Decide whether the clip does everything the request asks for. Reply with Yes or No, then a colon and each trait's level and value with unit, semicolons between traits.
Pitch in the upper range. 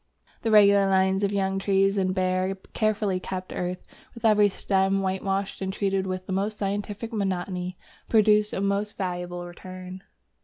Yes: high, 195 Hz